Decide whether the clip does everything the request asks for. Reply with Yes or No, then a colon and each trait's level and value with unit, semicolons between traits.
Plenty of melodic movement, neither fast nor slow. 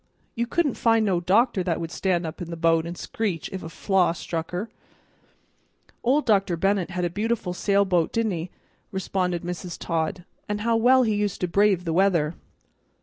No: average, 3.5 semitones; average, 185 wpm